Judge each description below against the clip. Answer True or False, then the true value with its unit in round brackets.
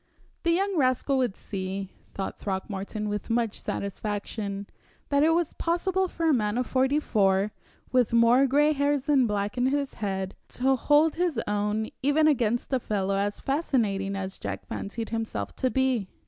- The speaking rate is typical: True (165 wpm)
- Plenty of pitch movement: True (5.8 semitones)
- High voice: True (235 Hz)